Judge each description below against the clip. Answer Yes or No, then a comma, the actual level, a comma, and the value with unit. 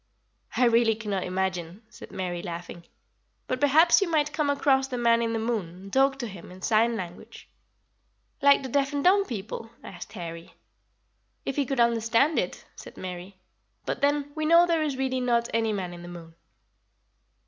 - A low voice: No, high, 230 Hz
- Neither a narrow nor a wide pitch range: No, wide, 6.8 semitones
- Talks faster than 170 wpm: Yes, average, 180 wpm